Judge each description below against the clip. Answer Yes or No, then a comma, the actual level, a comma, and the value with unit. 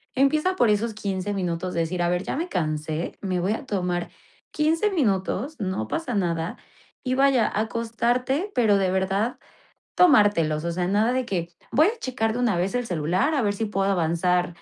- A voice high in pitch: Yes, high, 205 Hz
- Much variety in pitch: Yes, wide, 5.9 semitones